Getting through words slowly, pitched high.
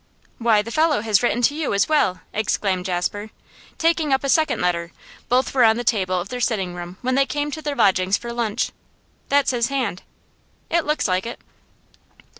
No: average, 195 wpm; high, 235 Hz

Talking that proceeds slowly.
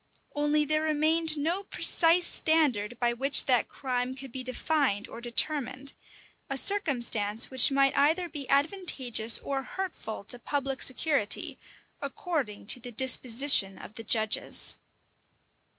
Yes: slow, 130 wpm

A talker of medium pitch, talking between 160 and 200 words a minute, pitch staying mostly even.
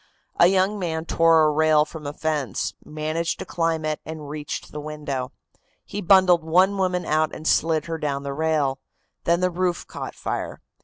Yes: medium, 160 Hz; average, 185 wpm; narrow, 2.2 semitones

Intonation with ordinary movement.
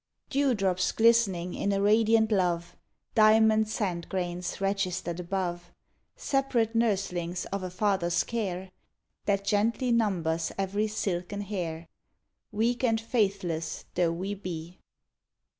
Yes: average, 3.7 semitones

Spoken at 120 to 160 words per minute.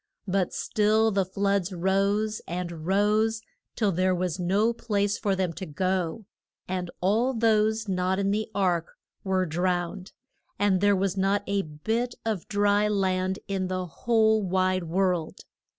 Yes: average, 150 wpm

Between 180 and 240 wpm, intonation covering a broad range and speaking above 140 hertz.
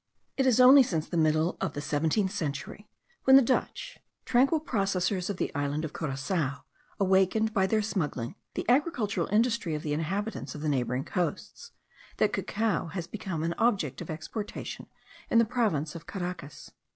No: average, 165 wpm; wide, 6.0 semitones; medium, 185 Hz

